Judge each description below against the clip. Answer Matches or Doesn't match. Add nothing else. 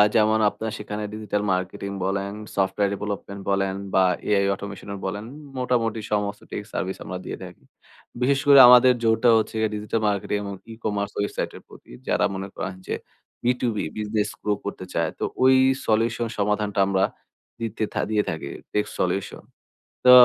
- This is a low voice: Matches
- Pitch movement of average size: Doesn't match